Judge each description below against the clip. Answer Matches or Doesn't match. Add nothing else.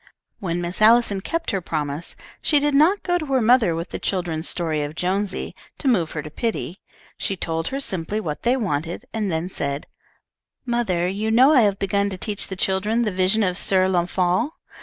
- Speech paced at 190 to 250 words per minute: Matches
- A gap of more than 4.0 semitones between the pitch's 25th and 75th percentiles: Matches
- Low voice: Doesn't match